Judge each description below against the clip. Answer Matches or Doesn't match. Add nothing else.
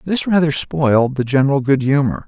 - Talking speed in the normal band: Matches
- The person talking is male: Matches